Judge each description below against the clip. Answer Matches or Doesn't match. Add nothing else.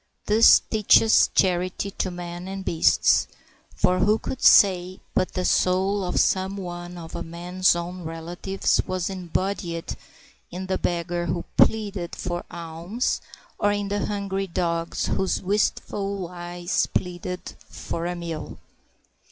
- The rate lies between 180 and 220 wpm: Doesn't match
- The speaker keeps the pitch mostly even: Matches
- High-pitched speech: Doesn't match